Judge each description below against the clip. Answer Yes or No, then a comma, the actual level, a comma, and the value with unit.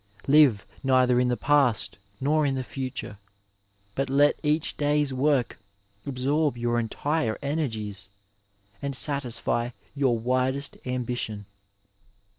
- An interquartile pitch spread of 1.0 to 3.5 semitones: Yes, average, 3.2 semitones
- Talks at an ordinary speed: No, slow, 110 wpm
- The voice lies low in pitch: Yes, low, 130 Hz